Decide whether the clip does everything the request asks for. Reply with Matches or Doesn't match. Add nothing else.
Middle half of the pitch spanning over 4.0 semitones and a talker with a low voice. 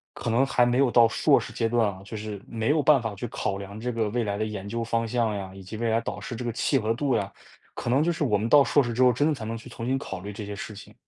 Doesn't match